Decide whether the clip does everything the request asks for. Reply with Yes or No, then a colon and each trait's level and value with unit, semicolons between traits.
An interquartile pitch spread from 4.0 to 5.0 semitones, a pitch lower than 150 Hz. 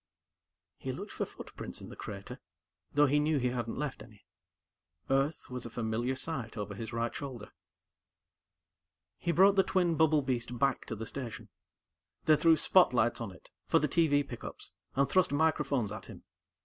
Yes: average, 4.5 semitones; low, 135 Hz